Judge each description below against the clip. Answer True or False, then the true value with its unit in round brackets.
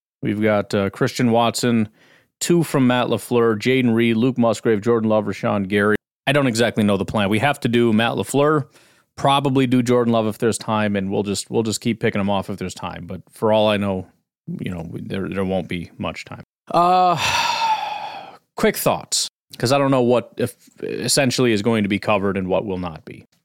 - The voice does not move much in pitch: False (4.2 semitones)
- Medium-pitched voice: False (115 Hz)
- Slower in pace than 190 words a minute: False (205 wpm)